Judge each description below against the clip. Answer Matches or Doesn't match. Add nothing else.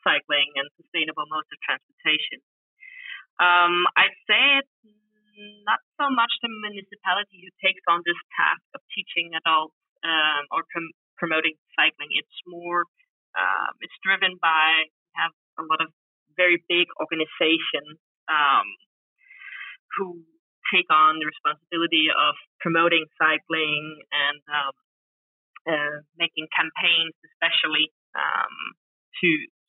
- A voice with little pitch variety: Doesn't match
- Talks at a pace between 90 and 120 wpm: Matches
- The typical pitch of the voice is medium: Matches